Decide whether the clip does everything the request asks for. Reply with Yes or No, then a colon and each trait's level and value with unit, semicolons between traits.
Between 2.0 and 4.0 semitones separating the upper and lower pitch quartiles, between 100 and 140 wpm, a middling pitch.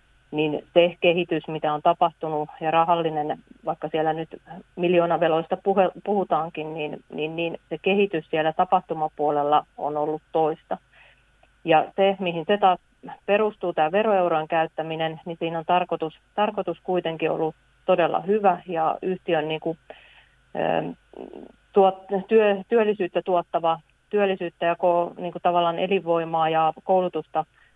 Yes: average, 2.8 semitones; average, 125 wpm; medium, 170 Hz